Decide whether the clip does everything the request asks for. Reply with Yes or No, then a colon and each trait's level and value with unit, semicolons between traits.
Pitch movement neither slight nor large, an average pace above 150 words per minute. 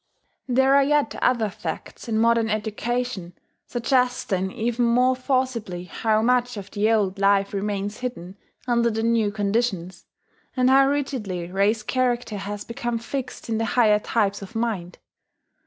No: average, 3.5 semitones; average, 145 wpm